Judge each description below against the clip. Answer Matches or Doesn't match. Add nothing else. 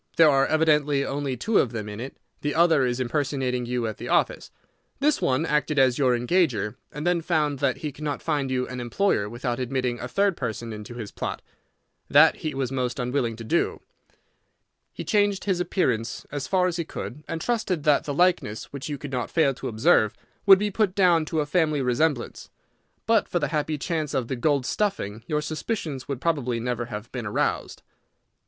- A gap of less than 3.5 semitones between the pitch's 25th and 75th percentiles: Doesn't match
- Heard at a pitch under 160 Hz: Matches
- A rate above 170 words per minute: Matches